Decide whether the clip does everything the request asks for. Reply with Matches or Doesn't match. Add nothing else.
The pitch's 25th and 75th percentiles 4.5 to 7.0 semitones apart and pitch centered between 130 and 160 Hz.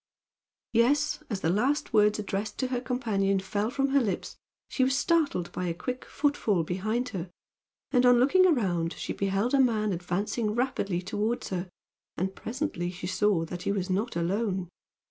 Doesn't match